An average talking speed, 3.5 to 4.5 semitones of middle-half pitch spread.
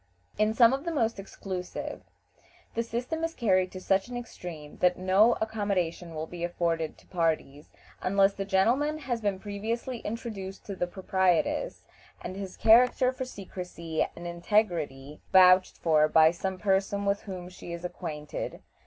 Yes: average, 155 wpm; average, 4.2 semitones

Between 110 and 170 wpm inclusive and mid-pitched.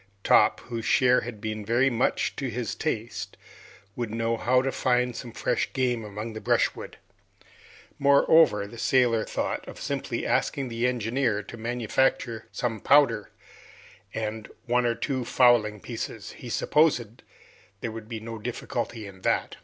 No: average, 150 wpm; low, 120 Hz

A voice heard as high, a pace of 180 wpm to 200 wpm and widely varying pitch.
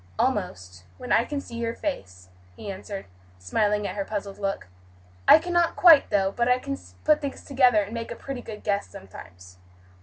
Yes: high, 210 Hz; average, 185 wpm; wide, 5.7 semitones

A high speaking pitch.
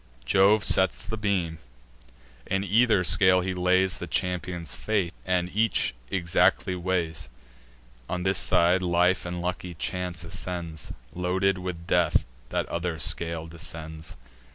No: very low, 90 Hz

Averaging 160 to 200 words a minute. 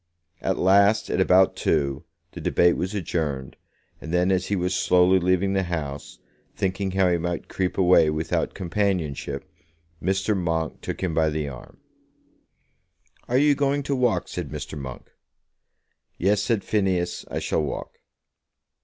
No: average, 150 wpm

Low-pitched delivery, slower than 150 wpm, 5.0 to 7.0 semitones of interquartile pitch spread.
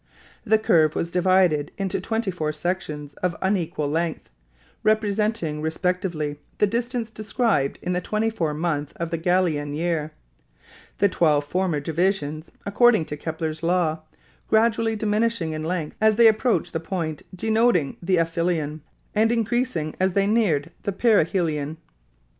No: medium, 175 Hz; average, 140 wpm; average, 5.3 semitones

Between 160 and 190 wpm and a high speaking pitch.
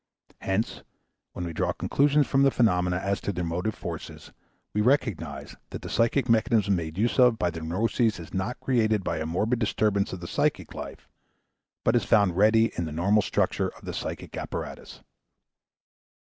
No: average, 175 wpm; low, 105 Hz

